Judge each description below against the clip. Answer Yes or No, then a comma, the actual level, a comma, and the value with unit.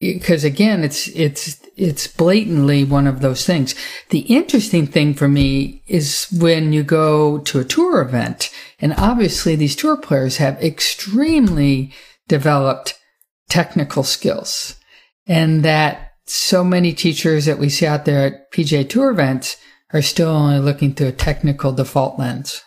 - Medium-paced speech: Yes, average, 150 wpm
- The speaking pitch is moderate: Yes, medium, 155 Hz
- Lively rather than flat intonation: No, average, 3.7 semitones